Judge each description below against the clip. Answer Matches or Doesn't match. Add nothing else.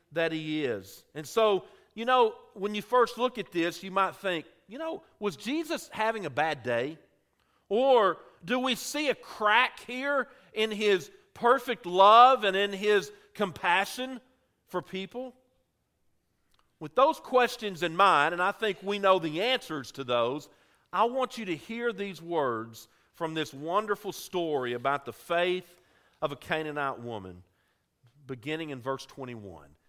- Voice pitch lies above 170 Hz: Matches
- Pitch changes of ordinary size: Doesn't match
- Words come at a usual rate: Matches